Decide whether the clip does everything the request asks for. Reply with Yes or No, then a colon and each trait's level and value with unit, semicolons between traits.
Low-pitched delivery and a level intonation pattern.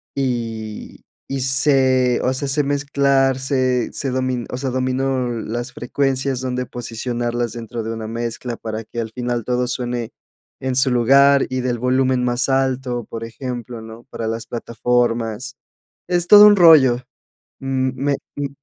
Yes: low, 125 Hz; narrow, 2.1 semitones